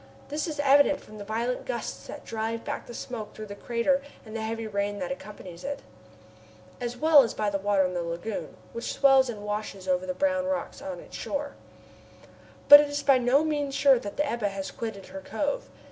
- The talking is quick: Yes, fast, 210 wpm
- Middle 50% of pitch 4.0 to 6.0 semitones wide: Yes, wide, 5.5 semitones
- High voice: Yes, high, 235 Hz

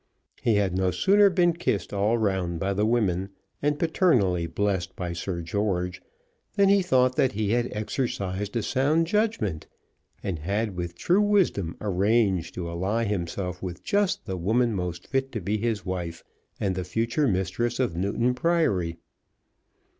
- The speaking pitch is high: No, low, 100 Hz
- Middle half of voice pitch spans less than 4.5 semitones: No, wide, 5.5 semitones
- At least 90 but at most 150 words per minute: No, average, 160 wpm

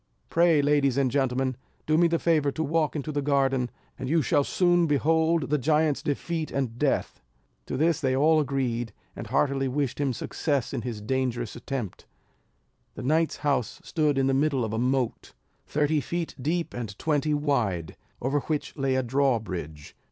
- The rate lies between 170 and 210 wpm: Yes, average, 175 wpm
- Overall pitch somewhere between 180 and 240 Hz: No, medium, 140 Hz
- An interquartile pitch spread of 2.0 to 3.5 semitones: Yes, average, 3.2 semitones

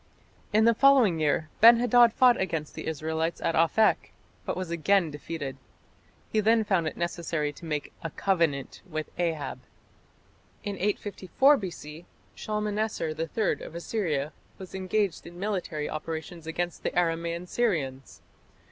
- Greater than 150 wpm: No, average, 140 wpm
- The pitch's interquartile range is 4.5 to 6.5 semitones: Yes, average, 4.8 semitones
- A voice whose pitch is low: No, medium, 170 Hz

